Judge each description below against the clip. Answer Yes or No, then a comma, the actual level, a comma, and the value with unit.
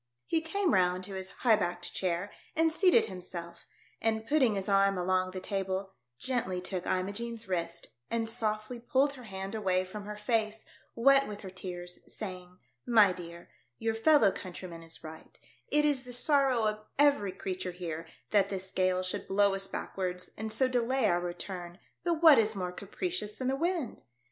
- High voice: Yes, high, 200 Hz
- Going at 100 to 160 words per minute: No, average, 180 wpm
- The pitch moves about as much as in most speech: Yes, average, 4.4 semitones